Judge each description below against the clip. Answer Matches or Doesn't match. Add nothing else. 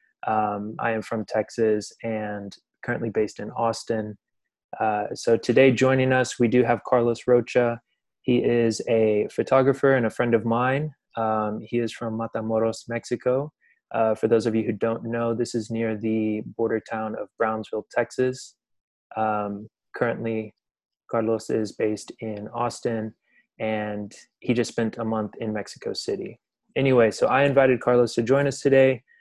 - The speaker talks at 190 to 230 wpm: Doesn't match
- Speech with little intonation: Matches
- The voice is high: Doesn't match